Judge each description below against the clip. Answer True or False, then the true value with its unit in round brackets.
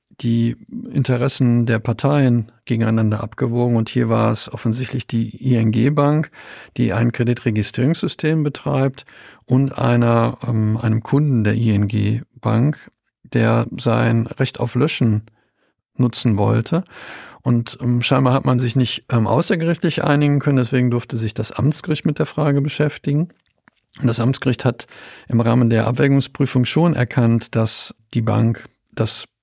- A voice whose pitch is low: True (125 Hz)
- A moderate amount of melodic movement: True (3.3 semitones)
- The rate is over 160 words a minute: False (135 wpm)